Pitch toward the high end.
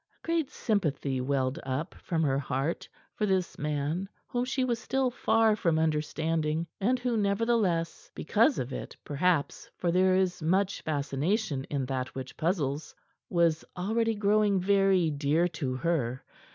No: medium, 170 Hz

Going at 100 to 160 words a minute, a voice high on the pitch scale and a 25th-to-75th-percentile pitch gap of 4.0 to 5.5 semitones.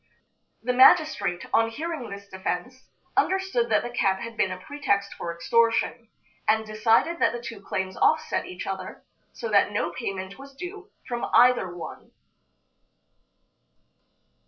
Yes: average, 140 wpm; high, 225 Hz; average, 5.2 semitones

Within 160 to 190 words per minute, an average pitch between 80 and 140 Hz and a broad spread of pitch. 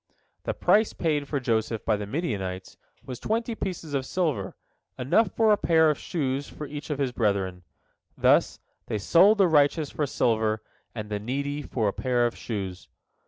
Yes: average, 180 wpm; low, 135 Hz; wide, 6.8 semitones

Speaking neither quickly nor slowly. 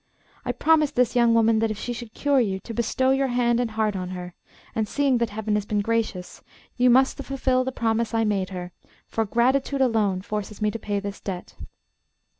No: fast, 210 wpm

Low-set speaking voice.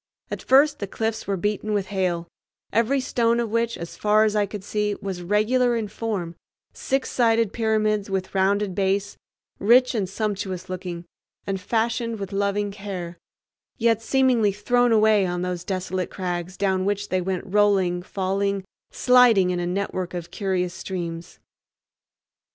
No: high, 200 Hz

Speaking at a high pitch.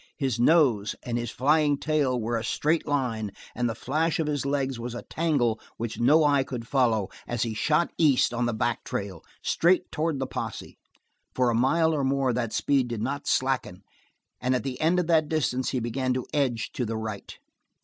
No: low, 130 Hz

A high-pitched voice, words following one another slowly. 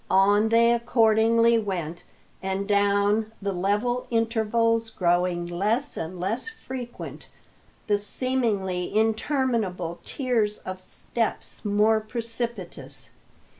Yes: high, 215 Hz; slow, 95 wpm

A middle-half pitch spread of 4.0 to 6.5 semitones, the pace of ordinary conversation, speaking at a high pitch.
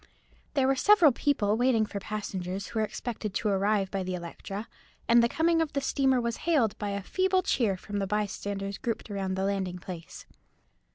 Yes: average, 4.6 semitones; average, 190 wpm; high, 210 Hz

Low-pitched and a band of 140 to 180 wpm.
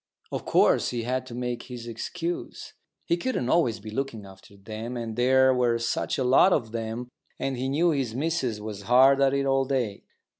No: low, 125 Hz; average, 195 wpm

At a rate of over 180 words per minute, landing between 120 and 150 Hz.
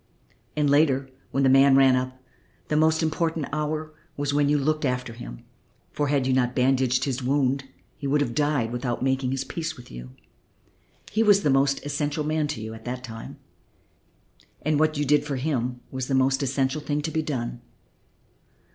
Yes: average, 190 wpm; medium, 140 Hz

